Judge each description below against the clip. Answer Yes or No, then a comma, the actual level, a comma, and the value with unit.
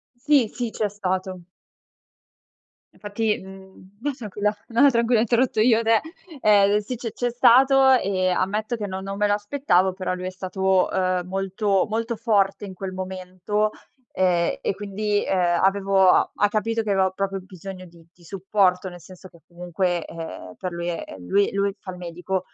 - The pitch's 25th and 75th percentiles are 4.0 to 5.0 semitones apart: No, narrow, 2.6 semitones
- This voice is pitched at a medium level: No, high, 195 Hz